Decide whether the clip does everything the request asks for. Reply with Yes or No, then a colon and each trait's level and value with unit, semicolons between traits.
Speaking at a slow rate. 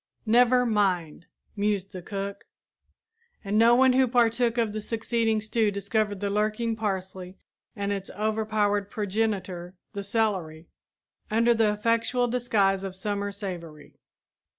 Yes: slow, 130 wpm